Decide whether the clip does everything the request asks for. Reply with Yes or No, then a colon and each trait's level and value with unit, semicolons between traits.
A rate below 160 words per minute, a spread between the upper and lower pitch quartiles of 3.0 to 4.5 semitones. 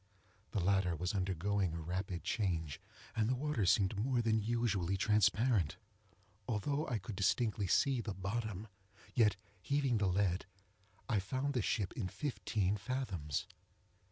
Yes: average, 140 wpm; average, 4.0 semitones